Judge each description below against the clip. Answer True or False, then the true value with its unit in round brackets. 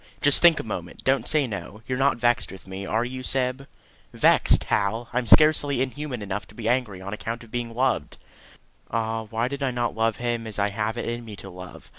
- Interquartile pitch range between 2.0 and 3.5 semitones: True (3.2 semitones)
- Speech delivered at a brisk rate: True (230 wpm)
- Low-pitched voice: True (115 Hz)